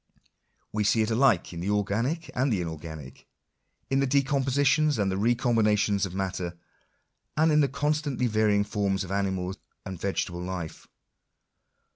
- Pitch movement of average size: No, wide, 6.0 semitones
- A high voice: No, low, 105 Hz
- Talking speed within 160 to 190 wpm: No, average, 150 wpm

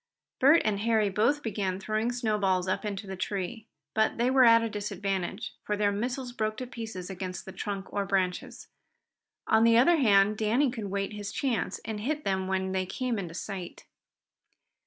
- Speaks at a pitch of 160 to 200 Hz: No, high, 210 Hz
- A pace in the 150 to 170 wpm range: No, average, 180 wpm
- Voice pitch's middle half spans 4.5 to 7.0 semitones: No, average, 3.1 semitones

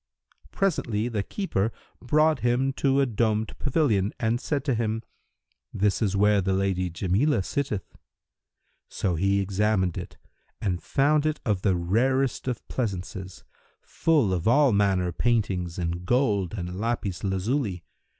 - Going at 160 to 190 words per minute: No, average, 140 wpm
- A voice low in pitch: Yes, low, 105 Hz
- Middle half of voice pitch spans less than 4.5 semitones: No, average, 5.2 semitones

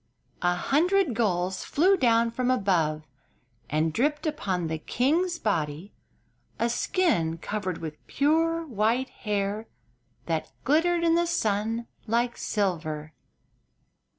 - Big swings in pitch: Yes, wide, 8.9 semitones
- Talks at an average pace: No, slow, 115 wpm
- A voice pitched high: Yes, high, 225 Hz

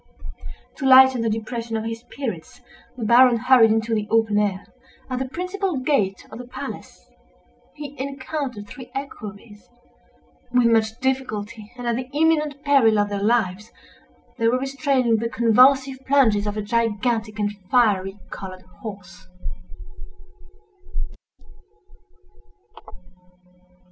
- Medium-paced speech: No, slow, 125 wpm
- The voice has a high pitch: Yes, high, 230 Hz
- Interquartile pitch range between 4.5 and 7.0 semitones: No, average, 3.8 semitones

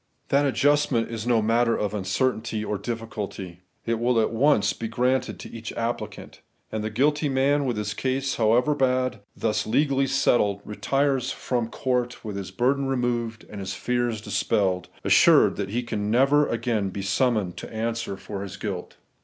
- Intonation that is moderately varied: Yes, average, 3.5 semitones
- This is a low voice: Yes, low, 115 Hz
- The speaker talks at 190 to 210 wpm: No, average, 170 wpm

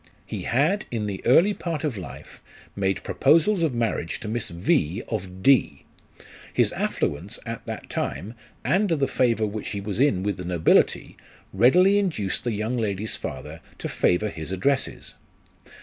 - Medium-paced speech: Yes, average, 165 wpm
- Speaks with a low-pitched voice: Yes, low, 110 Hz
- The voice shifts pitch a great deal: Yes, wide, 6.6 semitones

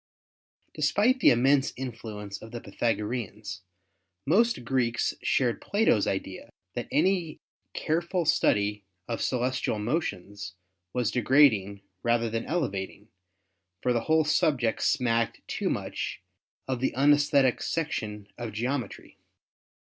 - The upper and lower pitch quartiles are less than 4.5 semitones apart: No, average, 5.3 semitones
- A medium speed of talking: No, slow, 110 wpm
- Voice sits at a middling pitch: No, low, 120 Hz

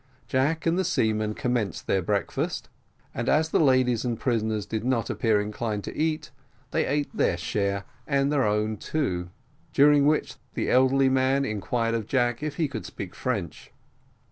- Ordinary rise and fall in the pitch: Yes, average, 4.6 semitones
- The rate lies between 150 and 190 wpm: Yes, average, 170 wpm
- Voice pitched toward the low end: Yes, low, 125 Hz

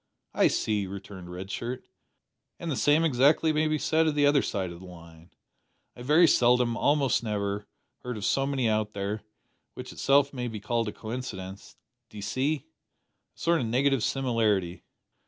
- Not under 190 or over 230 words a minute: No, average, 175 wpm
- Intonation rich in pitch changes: Yes, wide, 5.7 semitones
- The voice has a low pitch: Yes, low, 120 Hz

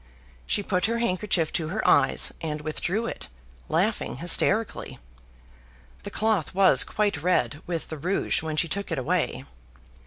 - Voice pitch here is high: No, medium, 180 Hz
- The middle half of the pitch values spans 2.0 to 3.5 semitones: No, average, 4.7 semitones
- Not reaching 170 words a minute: Yes, average, 150 wpm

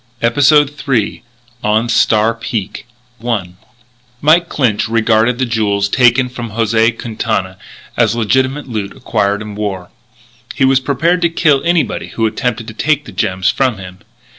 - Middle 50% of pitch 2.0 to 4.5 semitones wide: Yes, average, 3.8 semitones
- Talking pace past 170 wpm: No, average, 145 wpm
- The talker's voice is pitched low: Yes, low, 115 Hz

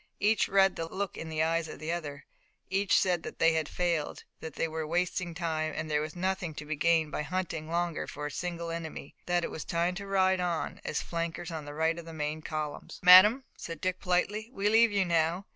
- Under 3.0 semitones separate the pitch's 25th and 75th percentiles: Yes, narrow, 2.6 semitones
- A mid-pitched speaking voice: Yes, medium, 170 Hz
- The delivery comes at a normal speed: No, fast, 230 wpm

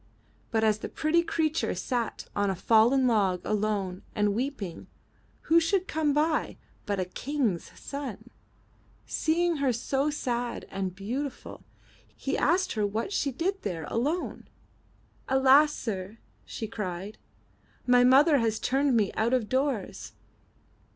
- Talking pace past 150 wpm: No, slow, 135 wpm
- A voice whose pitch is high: Yes, high, 245 Hz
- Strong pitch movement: Yes, wide, 5.7 semitones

